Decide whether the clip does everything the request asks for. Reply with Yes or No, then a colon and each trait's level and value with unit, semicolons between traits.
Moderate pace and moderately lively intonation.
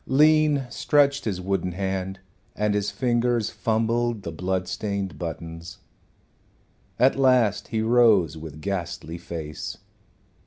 No: slow, 115 wpm; average, 4.9 semitones